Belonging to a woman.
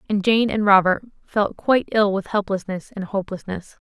Yes: female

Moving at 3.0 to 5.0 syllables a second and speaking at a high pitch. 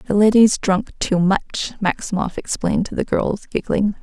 Yes: 4.8 syllables/s; high, 200 Hz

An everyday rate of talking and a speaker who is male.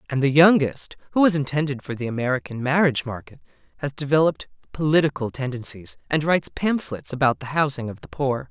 Yes: average, 170 wpm; male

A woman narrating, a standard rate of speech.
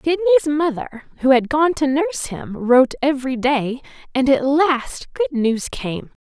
Yes: female; average, 165 wpm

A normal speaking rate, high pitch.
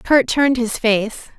Yes: average, 175 wpm; high, 240 Hz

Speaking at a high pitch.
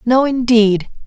Yes: high, 235 Hz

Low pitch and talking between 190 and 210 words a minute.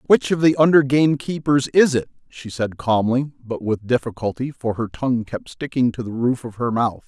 Yes: low, 125 Hz; fast, 205 wpm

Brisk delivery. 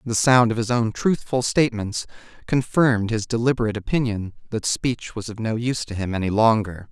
No: average, 180 wpm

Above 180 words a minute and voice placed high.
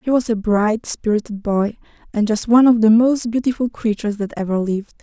Yes: fast, 205 wpm; high, 220 Hz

